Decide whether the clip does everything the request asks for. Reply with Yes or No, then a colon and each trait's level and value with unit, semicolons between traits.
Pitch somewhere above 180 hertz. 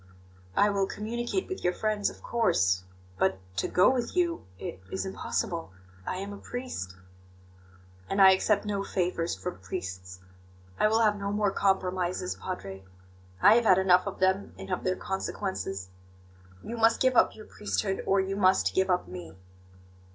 Yes: high, 190 Hz